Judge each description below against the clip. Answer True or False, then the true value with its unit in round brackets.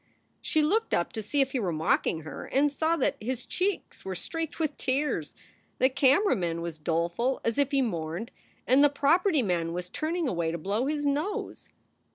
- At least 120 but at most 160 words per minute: False (195 wpm)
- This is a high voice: True (260 Hz)